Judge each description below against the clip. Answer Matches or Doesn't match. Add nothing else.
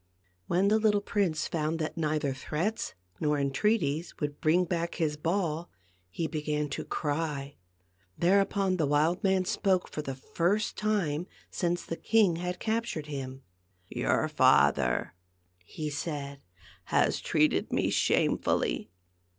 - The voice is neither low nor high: Matches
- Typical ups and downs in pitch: Matches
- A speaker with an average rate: Doesn't match